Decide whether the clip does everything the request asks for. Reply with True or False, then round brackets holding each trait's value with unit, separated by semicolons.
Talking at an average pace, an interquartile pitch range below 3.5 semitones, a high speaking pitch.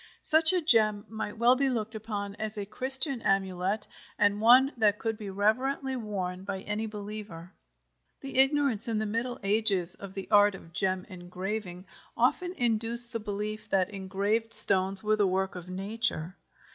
True (165 wpm; 2.9 semitones; 210 Hz)